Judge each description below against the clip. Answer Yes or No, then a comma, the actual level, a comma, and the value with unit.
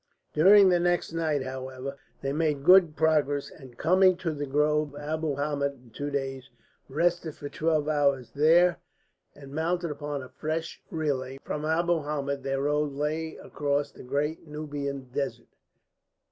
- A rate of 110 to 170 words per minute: Yes, average, 155 wpm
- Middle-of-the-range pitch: Yes, medium, 150 Hz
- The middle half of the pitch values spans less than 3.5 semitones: Yes, narrow, 2.4 semitones